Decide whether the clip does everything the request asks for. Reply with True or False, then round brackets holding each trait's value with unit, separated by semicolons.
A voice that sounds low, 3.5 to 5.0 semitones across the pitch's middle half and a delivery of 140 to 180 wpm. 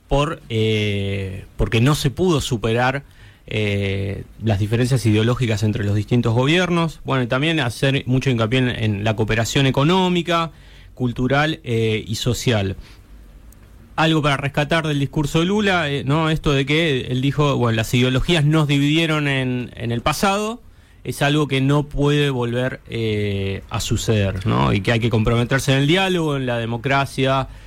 True (130 Hz; 4.7 semitones; 160 wpm)